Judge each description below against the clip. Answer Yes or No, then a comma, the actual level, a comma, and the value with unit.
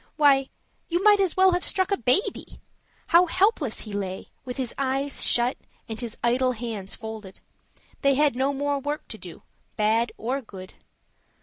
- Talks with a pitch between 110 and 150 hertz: No, very high, 265 Hz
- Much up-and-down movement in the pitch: No, average, 4.8 semitones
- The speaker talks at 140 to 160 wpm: No, average, 170 wpm